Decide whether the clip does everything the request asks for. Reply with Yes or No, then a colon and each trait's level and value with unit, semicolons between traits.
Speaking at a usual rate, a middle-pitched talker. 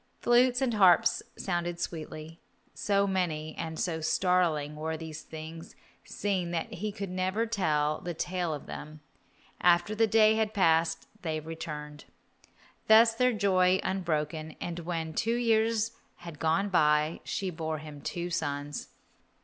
Yes: average, 145 wpm; medium, 170 Hz